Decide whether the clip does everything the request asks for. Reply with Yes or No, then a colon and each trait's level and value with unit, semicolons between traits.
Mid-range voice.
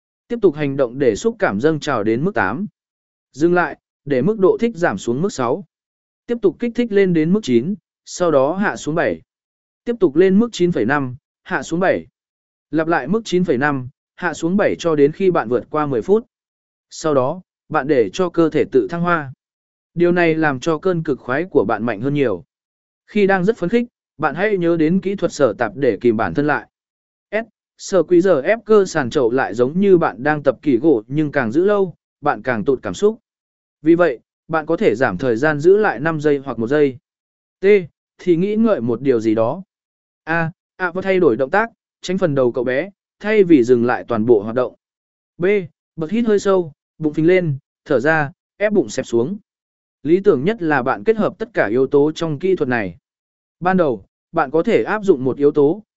Yes: medium, 175 Hz